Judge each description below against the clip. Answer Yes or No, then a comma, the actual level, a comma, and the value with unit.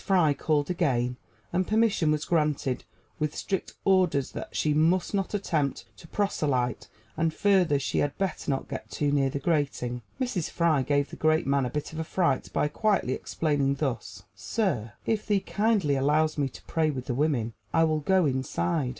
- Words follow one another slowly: No, average, 180 wpm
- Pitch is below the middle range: No, medium, 155 Hz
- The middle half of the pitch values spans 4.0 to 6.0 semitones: Yes, average, 4.5 semitones